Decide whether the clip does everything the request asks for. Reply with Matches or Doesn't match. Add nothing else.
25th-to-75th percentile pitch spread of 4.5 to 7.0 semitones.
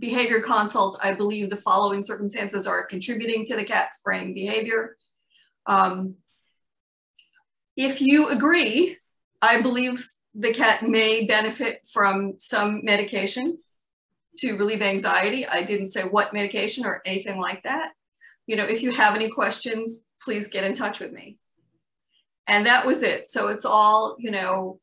Doesn't match